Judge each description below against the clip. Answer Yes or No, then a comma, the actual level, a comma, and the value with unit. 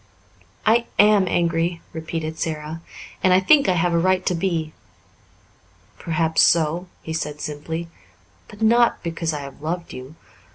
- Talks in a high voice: No, medium, 165 Hz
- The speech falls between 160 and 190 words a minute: No, average, 150 wpm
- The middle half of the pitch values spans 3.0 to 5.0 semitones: No, narrow, 2.6 semitones